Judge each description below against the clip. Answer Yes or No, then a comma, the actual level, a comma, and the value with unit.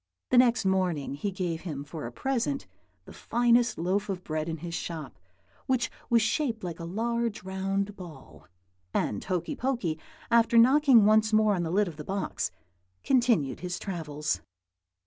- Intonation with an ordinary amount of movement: No, wide, 5.9 semitones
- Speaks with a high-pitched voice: Yes, high, 195 Hz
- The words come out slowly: No, average, 165 wpm